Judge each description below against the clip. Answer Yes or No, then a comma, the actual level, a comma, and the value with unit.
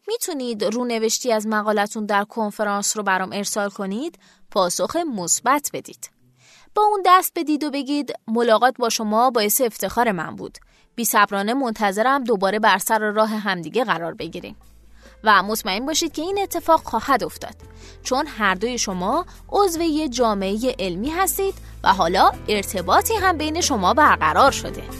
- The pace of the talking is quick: No, average, 145 wpm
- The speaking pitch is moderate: No, high, 230 Hz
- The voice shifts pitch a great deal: Yes, wide, 6.8 semitones